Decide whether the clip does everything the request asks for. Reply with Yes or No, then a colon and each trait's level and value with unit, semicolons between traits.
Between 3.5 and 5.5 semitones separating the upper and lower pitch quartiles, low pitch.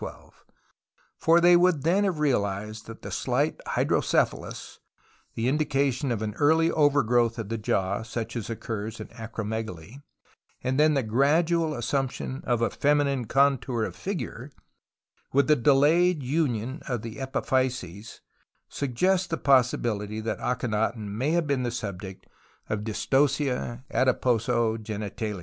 Yes: average, 4.5 semitones; low, 125 Hz